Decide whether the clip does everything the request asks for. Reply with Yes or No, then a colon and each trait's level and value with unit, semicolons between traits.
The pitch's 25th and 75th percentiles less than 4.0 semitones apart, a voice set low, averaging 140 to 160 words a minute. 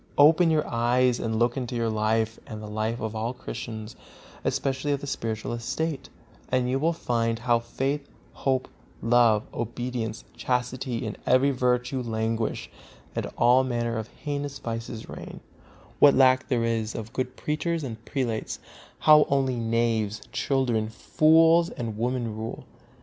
Yes: average, 2.8 semitones; low, 120 Hz; average, 150 wpm